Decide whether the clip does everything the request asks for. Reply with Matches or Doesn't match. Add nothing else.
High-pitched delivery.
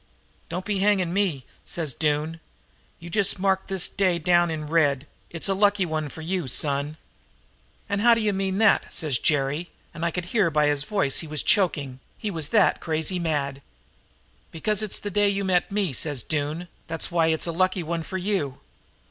Doesn't match